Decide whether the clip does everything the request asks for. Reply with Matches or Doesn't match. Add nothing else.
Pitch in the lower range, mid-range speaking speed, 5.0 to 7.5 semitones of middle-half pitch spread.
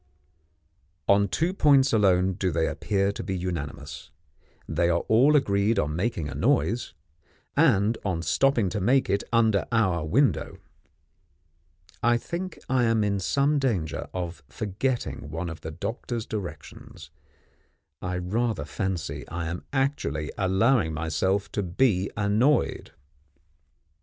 Doesn't match